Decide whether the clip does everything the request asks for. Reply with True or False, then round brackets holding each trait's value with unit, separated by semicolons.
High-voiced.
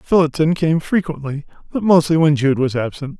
False (155 Hz)